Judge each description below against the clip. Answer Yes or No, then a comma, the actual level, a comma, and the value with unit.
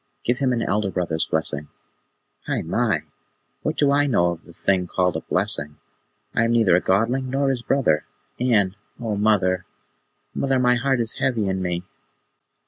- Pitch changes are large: Yes, wide, 5.7 semitones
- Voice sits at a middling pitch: No, low, 105 Hz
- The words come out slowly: No, average, 170 wpm